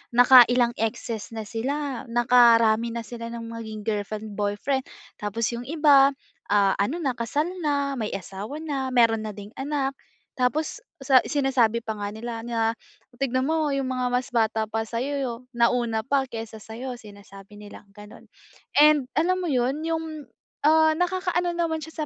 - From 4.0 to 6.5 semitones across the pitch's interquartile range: Yes, average, 4.3 semitones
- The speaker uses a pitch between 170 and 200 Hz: No, high, 245 Hz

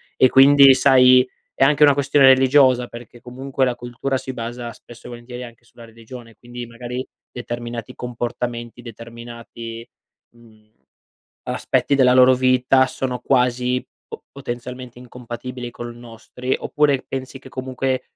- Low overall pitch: Yes, low, 125 Hz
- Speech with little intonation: Yes, narrow, 1.7 semitones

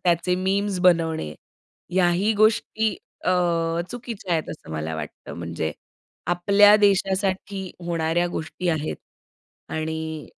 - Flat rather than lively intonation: No, average, 3.7 semitones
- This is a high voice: No, medium, 175 Hz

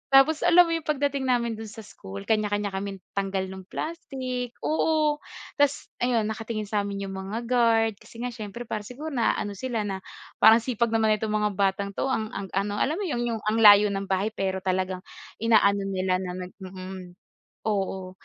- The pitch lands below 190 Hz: No, high, 215 Hz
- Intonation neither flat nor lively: Yes, average, 3.8 semitones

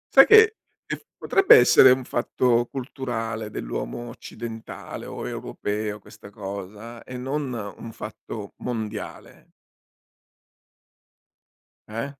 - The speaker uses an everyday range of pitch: Yes, average, 3.1 semitones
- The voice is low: Yes, low, 115 Hz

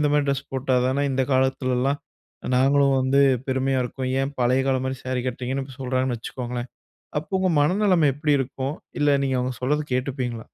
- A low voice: Yes, low, 130 Hz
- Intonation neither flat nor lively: No, narrow, 1.7 semitones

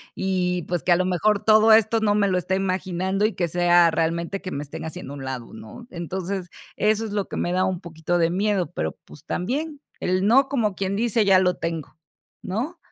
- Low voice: No, medium, 185 Hz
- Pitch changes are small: No, average, 3.3 semitones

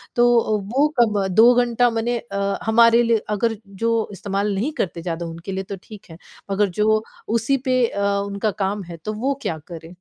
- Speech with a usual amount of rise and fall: Yes, average, 3.0 semitones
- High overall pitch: Yes, high, 210 Hz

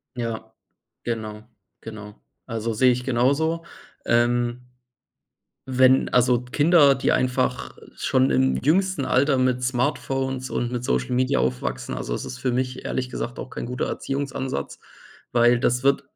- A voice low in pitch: Yes, low, 125 Hz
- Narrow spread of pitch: Yes, narrow, 1.9 semitones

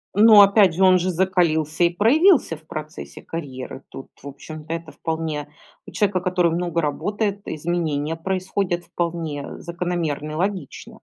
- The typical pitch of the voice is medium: Yes, medium, 170 Hz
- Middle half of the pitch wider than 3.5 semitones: No, average, 3.2 semitones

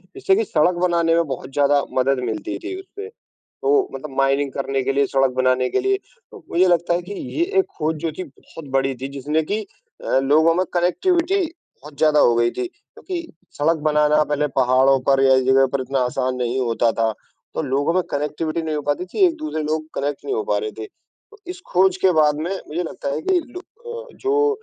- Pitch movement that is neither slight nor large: No, wide, 5.8 semitones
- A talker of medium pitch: Yes, medium, 155 Hz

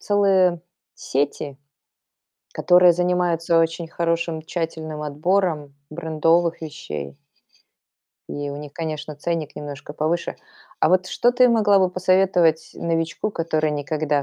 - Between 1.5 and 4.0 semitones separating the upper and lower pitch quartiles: Yes, average, 2.8 semitones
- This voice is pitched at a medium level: Yes, medium, 165 Hz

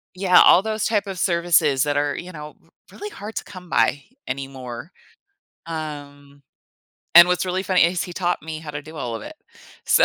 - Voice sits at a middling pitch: Yes, medium, 165 Hz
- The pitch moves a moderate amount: Yes, average, 4.1 semitones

